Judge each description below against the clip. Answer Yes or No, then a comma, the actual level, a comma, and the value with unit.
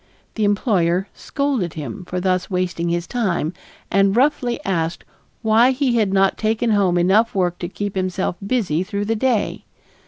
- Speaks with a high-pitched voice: Yes, high, 195 Hz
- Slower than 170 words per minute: Yes, average, 160 wpm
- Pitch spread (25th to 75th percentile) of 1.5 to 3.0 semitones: No, average, 3.9 semitones